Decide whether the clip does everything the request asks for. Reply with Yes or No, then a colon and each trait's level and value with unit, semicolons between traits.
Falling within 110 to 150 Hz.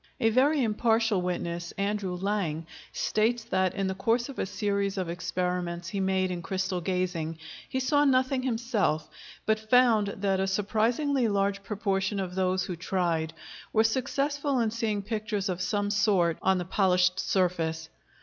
No: high, 195 Hz